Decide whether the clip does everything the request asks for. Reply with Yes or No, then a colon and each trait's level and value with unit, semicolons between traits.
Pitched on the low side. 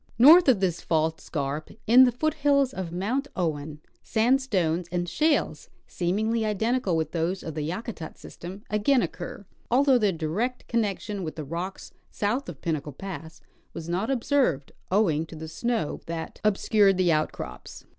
No: high, 190 Hz